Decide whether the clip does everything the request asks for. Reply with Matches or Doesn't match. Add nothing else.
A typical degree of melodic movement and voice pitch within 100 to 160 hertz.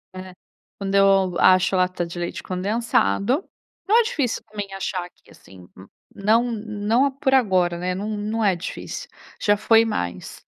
Doesn't match